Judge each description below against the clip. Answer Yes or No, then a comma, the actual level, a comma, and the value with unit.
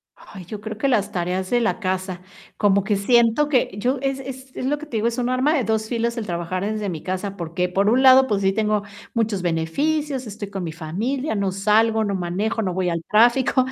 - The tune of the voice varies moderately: Yes, average, 4.8 semitones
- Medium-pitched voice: No, high, 215 Hz